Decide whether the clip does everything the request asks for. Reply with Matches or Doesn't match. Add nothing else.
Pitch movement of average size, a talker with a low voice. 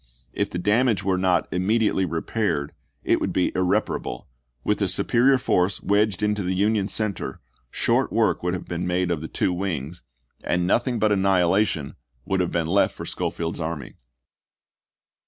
Matches